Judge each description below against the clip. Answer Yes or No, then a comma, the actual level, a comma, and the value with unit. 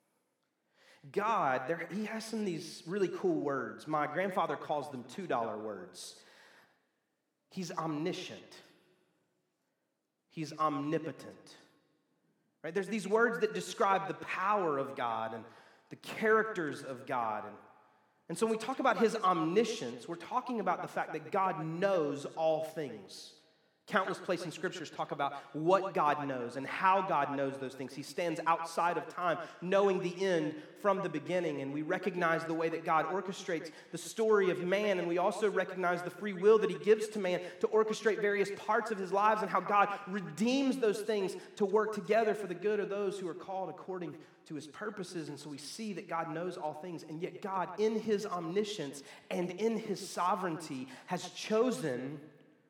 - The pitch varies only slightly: No, average, 4.6 semitones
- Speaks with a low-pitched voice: No, medium, 185 Hz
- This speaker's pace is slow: No, average, 175 wpm